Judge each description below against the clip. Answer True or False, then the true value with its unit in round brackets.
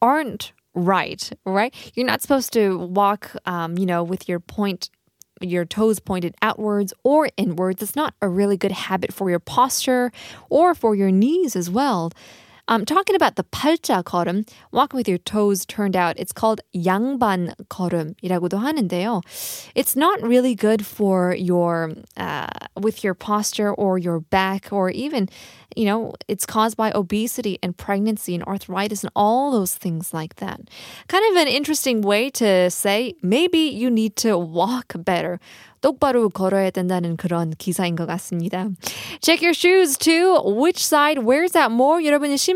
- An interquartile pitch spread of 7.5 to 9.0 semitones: False (5.5 semitones)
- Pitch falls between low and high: False (205 Hz)